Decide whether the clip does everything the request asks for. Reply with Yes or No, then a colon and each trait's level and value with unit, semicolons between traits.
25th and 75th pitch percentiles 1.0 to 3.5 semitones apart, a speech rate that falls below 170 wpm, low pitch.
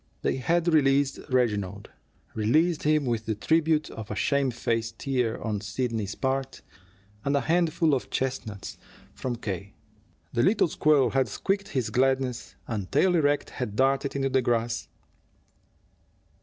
No: average, 4.3 semitones; average, 140 wpm; low, 130 Hz